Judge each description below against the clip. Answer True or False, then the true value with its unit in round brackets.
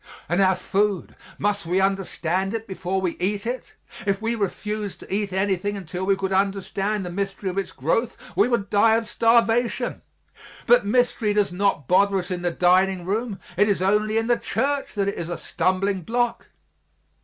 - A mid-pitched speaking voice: False (200 Hz)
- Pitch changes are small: True (2.3 semitones)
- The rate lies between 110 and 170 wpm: False (185 wpm)